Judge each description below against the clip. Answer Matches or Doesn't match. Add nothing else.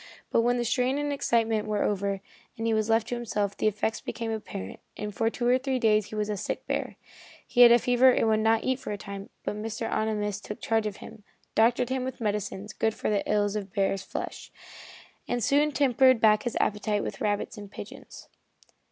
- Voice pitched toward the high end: Matches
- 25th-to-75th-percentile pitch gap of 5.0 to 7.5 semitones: Doesn't match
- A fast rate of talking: Matches